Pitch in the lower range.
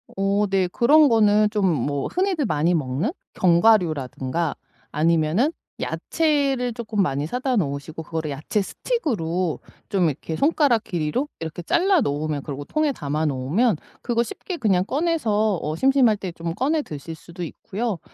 No: high, 195 Hz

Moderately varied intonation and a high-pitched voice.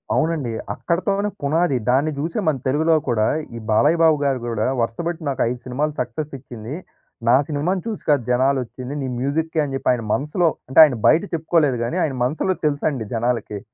No: average, 4.4 semitones; medium, 145 Hz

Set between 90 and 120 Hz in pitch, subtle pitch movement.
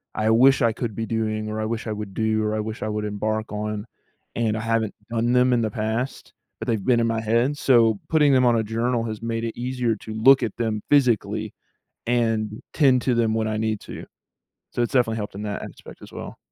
Yes: low, 115 Hz; narrow, 1.8 semitones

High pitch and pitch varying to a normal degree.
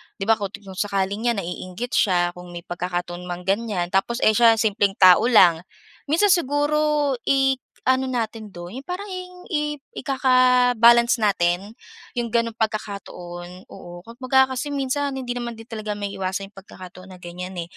No: high, 220 Hz; wide, 5.9 semitones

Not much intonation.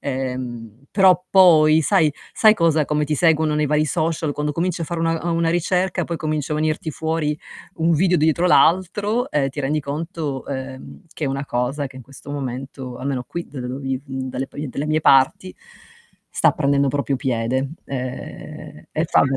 No: average, 3.5 semitones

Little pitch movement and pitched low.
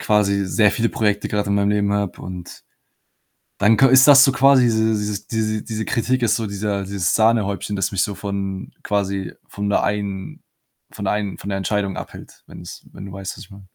Yes: narrow, 2.0 semitones; low, 100 Hz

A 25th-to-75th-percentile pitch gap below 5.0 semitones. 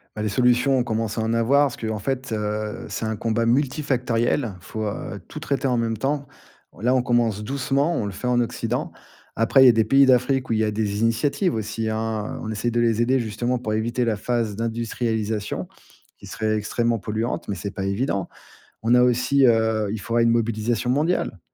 Yes: narrow, 2.4 semitones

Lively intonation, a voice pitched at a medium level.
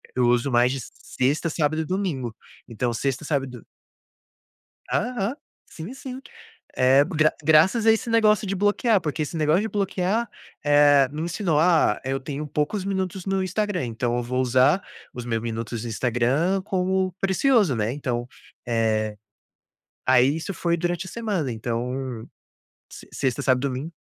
Yes: wide, 7.1 semitones; medium, 150 Hz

